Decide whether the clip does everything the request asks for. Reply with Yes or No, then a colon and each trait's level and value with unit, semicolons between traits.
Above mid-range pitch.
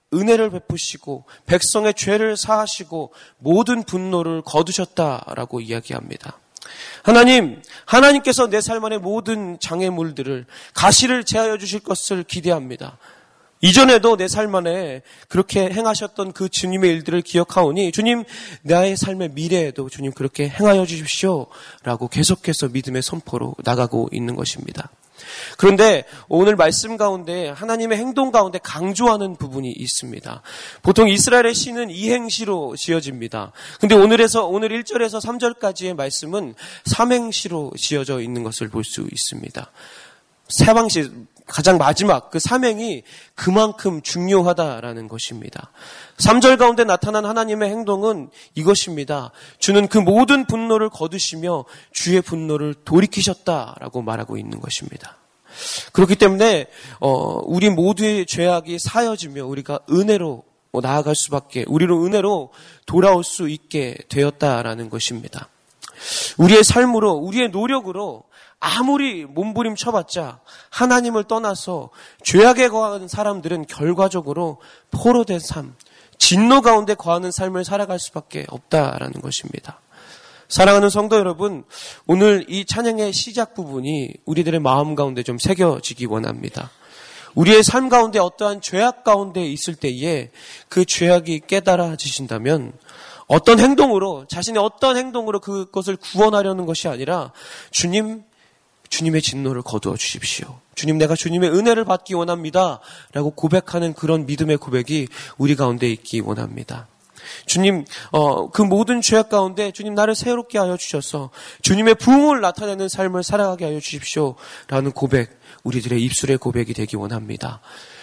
No: medium, 180 Hz